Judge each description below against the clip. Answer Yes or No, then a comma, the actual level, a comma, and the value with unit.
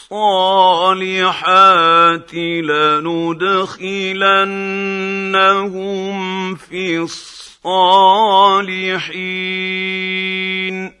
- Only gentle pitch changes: Yes, narrow, 0.8 semitones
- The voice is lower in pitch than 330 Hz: Yes, high, 190 Hz